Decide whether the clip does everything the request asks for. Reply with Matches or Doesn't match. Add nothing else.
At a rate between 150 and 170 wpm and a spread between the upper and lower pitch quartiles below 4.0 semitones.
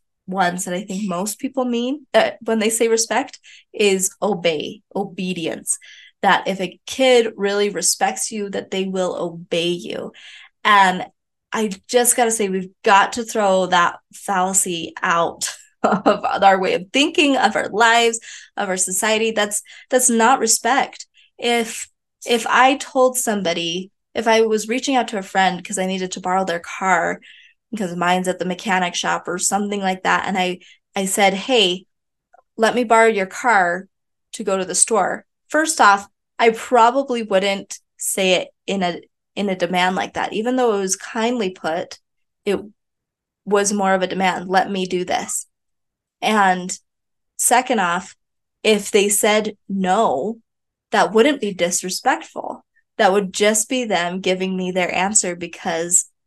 Matches